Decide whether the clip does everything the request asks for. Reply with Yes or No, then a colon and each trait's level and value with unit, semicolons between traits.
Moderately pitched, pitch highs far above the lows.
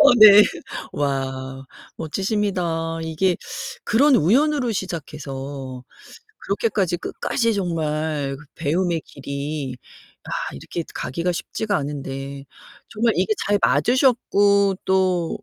Yes: medium, 170 Hz; wide, 6.1 semitones